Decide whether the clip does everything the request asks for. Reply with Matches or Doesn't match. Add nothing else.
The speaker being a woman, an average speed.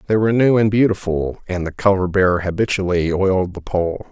Doesn't match